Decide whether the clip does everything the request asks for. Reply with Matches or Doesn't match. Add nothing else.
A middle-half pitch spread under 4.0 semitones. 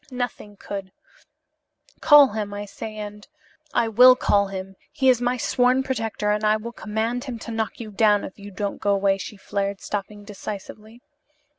Matches